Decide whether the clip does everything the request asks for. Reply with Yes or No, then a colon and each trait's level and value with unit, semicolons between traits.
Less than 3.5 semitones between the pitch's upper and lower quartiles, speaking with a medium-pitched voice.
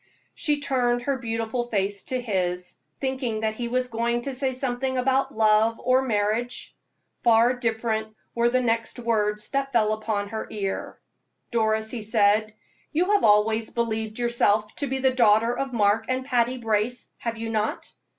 No: average, 2.7 semitones; high, 230 Hz